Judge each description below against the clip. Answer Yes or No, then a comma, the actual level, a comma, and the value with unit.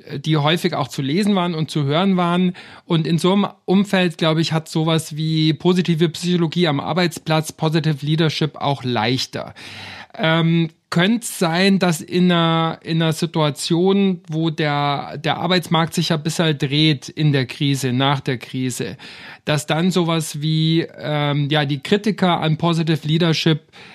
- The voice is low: No, medium, 165 Hz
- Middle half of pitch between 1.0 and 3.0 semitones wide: Yes, narrow, 2.6 semitones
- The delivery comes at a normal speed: Yes, average, 160 wpm